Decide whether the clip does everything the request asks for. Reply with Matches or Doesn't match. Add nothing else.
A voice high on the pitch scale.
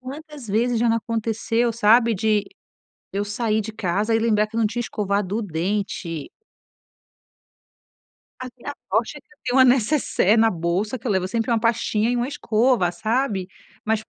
Matches